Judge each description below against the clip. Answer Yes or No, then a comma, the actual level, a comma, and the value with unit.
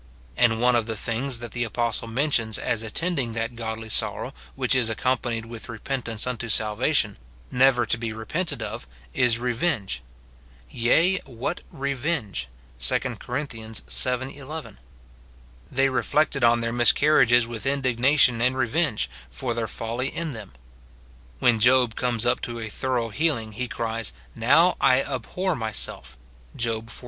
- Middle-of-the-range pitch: No, low, 120 Hz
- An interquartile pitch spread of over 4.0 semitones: No, average, 2.7 semitones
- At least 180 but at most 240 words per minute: No, average, 155 wpm